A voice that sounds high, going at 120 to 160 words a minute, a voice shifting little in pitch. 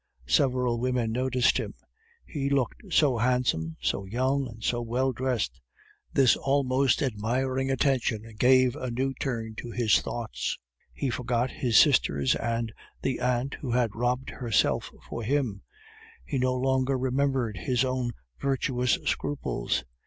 No: low, 125 Hz; average, 140 wpm; narrow, 2.3 semitones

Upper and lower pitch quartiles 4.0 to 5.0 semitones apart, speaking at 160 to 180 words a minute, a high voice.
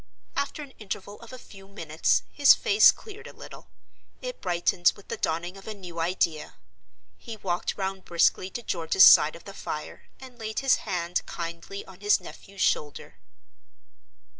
Yes: average, 4.5 semitones; average, 165 wpm; high, 195 Hz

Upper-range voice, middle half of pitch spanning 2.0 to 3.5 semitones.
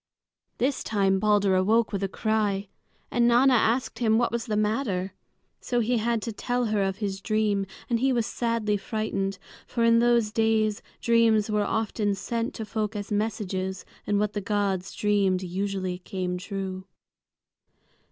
Yes: high, 210 Hz; average, 2.8 semitones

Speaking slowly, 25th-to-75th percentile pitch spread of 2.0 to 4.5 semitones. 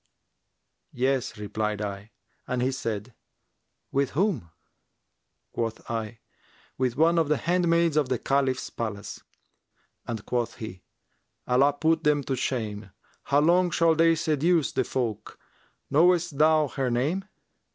No: slow, 130 wpm; wide, 5.6 semitones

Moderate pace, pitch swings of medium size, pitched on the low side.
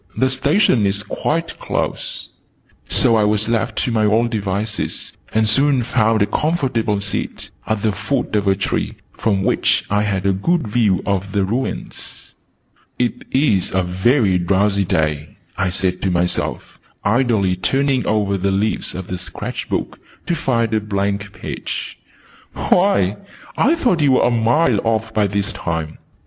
Yes: average, 160 wpm; average, 3.7 semitones; low, 105 Hz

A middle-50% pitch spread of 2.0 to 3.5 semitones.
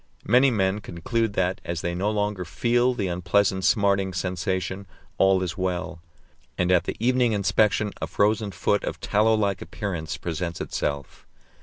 Yes: average, 2.9 semitones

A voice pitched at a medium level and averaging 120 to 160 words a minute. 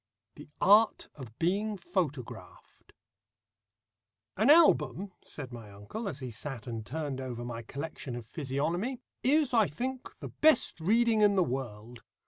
Yes: medium, 150 Hz; average, 140 wpm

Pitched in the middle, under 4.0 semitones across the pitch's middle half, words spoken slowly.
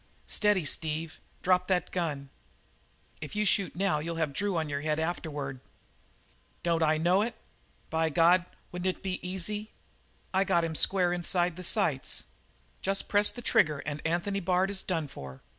No: medium, 175 Hz; average, 3.3 semitones; average, 165 wpm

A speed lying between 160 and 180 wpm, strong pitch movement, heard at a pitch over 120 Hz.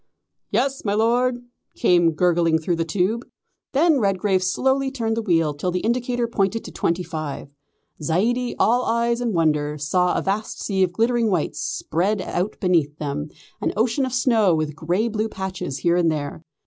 Yes: average, 175 wpm; wide, 5.9 semitones; high, 190 Hz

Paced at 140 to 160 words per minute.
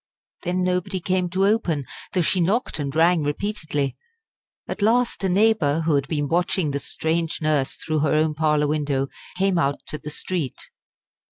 No: average, 170 wpm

